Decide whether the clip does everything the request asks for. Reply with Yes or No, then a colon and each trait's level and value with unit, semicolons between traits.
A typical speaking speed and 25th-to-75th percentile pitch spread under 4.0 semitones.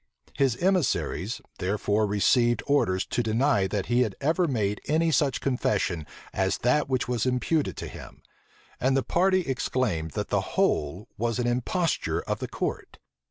No: average, 160 wpm; average, 5.3 semitones